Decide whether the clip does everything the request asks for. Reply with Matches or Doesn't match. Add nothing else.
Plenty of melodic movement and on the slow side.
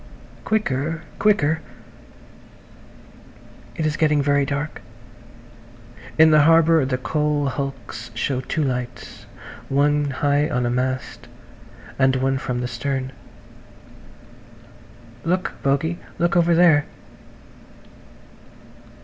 Doesn't match